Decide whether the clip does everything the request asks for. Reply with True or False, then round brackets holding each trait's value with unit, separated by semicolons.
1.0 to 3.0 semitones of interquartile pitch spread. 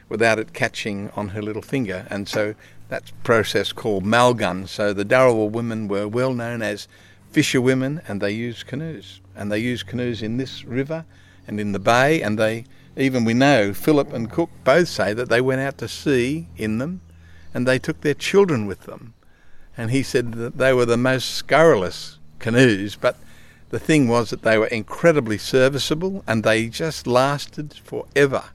False (4.1 semitones)